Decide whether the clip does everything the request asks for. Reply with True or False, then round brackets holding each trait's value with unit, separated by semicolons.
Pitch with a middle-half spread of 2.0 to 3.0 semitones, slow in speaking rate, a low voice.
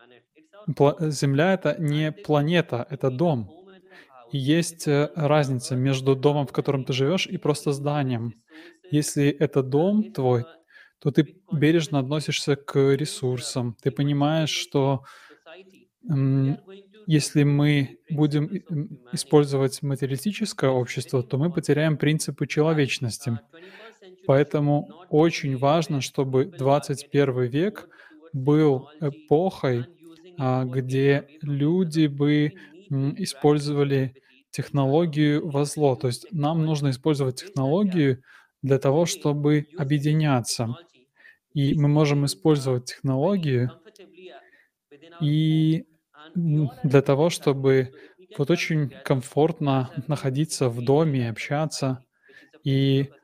False (2.6 semitones; 95 wpm; 145 Hz)